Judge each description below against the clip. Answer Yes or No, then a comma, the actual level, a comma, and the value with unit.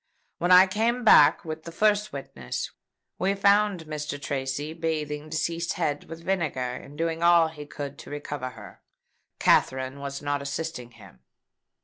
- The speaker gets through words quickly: No, average, 150 wpm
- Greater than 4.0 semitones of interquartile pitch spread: No, average, 3.3 semitones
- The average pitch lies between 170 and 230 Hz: No, medium, 155 Hz